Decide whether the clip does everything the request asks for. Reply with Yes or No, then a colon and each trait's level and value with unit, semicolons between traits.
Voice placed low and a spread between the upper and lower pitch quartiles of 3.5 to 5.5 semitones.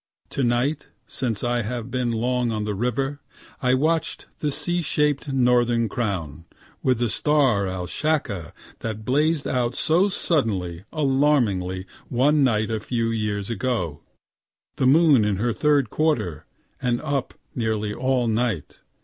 Yes: low, 120 Hz; average, 4.6 semitones